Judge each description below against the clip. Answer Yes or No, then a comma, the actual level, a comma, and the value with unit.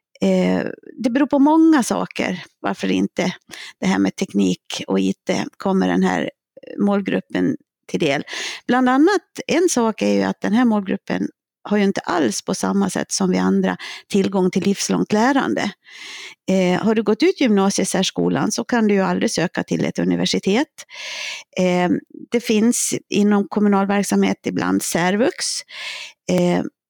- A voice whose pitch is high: Yes, high, 195 Hz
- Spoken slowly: No, average, 145 wpm